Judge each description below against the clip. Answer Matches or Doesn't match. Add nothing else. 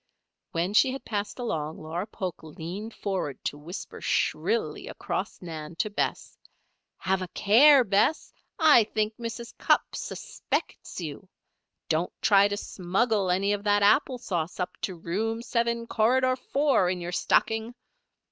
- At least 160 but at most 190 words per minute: Doesn't match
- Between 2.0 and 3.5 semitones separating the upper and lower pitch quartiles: Doesn't match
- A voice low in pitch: Doesn't match